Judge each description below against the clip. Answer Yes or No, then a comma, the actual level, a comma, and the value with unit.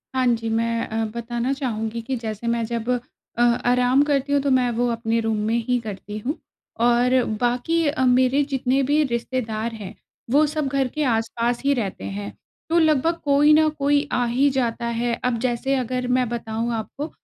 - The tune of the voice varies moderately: Yes, average, 3.1 semitones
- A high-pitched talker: Yes, high, 245 Hz